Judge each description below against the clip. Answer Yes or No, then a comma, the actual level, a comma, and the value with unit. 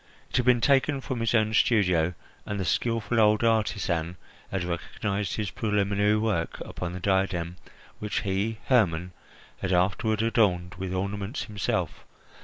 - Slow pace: No, average, 145 wpm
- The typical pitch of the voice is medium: No, low, 100 Hz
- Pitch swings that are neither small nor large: Yes, average, 3.3 semitones